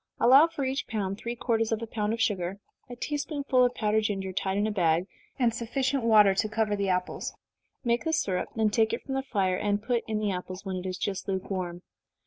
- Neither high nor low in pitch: No, high, 215 Hz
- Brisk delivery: Yes, fast, 230 wpm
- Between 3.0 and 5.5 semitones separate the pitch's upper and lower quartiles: Yes, average, 3.8 semitones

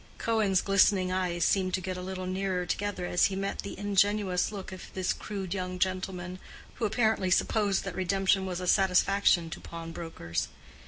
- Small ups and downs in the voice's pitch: Yes, narrow, 1.4 semitones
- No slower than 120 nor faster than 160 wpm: No, average, 170 wpm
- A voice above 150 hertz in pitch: Yes, medium, 185 Hz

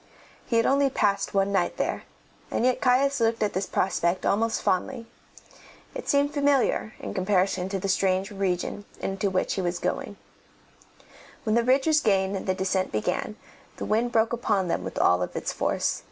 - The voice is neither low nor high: No, high, 200 Hz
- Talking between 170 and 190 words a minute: Yes, average, 180 wpm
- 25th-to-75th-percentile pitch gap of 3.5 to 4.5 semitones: Yes, average, 4.1 semitones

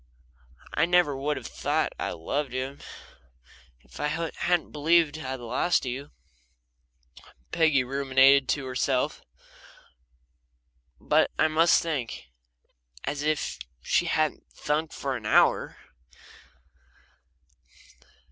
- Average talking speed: No, slow, 105 wpm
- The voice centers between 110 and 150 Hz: Yes, medium, 140 Hz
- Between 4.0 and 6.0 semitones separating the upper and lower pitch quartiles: No, average, 3.3 semitones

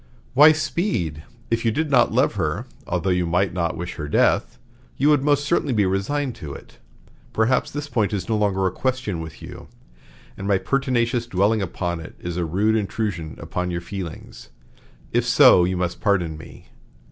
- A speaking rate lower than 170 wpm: No, average, 180 wpm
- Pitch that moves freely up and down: Yes, wide, 6.3 semitones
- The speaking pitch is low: Yes, low, 100 Hz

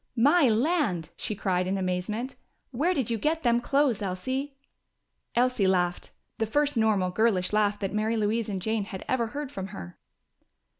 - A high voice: Yes, high, 220 Hz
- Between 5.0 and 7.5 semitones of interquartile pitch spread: Yes, average, 5.3 semitones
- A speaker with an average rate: Yes, average, 165 wpm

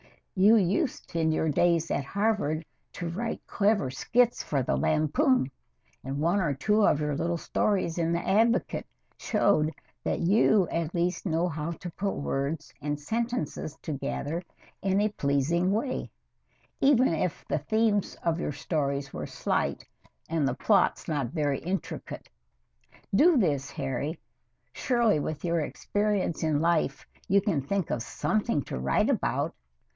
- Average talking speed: Yes, average, 150 wpm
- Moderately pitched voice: Yes, medium, 170 Hz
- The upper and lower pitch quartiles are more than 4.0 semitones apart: Yes, wide, 5.5 semitones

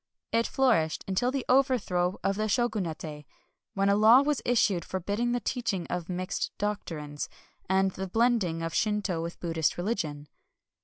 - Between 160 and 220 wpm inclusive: No, average, 150 wpm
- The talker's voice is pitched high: Yes, high, 195 Hz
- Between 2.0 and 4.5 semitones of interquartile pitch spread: No, wide, 5.4 semitones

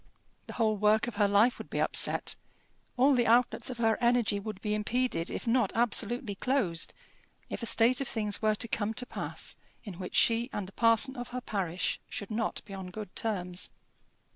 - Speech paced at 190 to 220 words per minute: Yes, average, 195 wpm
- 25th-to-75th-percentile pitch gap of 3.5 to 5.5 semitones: No, average, 3.0 semitones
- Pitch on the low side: No, high, 220 Hz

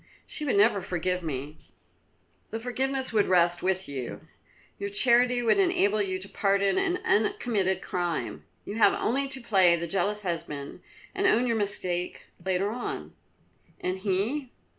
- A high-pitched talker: Yes, high, 200 Hz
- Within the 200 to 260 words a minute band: No, average, 150 wpm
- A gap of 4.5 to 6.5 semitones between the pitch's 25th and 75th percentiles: Yes, average, 4.8 semitones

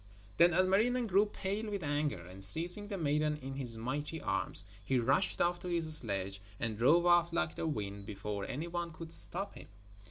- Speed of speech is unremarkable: Yes, average, 190 wpm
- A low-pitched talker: No, medium, 155 Hz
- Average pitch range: No, wide, 7.3 semitones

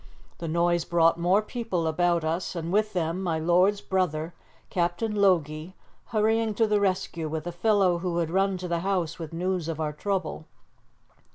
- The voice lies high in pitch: No, medium, 175 Hz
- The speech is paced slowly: No, average, 175 wpm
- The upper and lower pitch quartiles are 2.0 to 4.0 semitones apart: Yes, average, 2.9 semitones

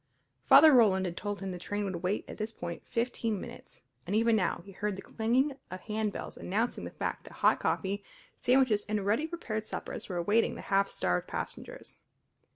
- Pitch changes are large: No, average, 3.1 semitones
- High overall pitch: Yes, high, 210 Hz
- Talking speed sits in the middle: Yes, average, 190 wpm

